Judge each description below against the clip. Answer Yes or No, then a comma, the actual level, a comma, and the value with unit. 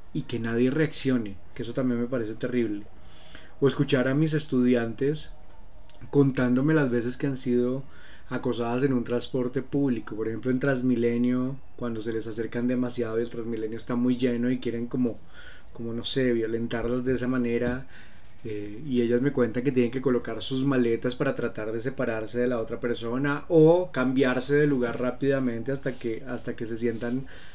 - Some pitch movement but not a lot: No, narrow, 2.2 semitones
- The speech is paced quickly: No, average, 175 wpm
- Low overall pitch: Yes, low, 125 Hz